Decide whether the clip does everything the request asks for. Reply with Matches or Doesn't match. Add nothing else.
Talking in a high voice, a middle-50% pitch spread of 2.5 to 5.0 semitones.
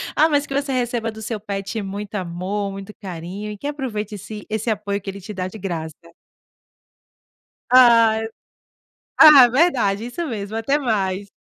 Matches